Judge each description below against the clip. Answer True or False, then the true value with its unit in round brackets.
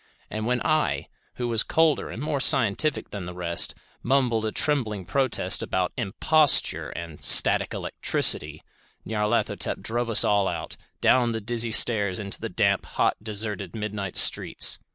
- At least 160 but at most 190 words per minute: False (150 wpm)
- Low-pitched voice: True (110 Hz)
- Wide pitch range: False (4.1 semitones)